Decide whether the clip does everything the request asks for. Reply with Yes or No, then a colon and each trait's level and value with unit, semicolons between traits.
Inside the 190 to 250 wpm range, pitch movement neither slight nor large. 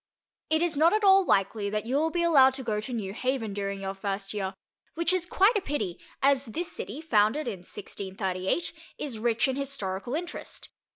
No: average, 195 wpm; wide, 7.9 semitones